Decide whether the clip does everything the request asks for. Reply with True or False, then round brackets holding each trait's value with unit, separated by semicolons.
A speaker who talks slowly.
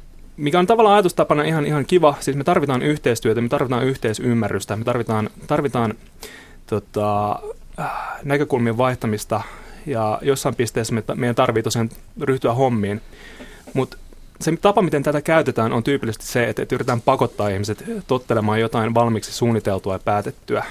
False (140 wpm)